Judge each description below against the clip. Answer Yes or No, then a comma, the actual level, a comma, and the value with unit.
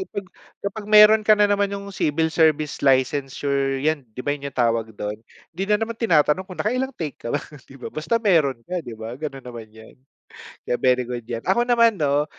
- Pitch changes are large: Yes, wide, 7.7 semitones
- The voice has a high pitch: No, medium, 150 Hz